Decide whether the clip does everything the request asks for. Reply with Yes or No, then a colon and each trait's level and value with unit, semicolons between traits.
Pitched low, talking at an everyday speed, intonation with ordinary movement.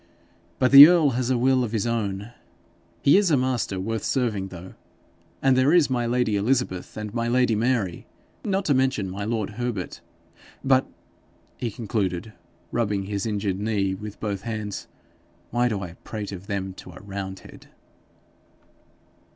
Yes: low, 110 Hz; average, 160 wpm; average, 4.2 semitones